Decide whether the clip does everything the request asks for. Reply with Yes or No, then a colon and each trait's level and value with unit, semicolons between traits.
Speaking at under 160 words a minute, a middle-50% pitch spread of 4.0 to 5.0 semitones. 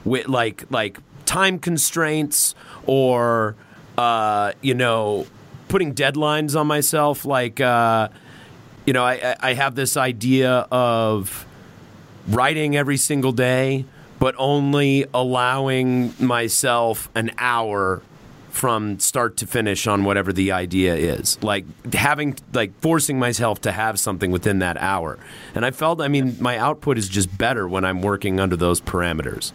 Yes: average, 140 wpm; average, 4.3 semitones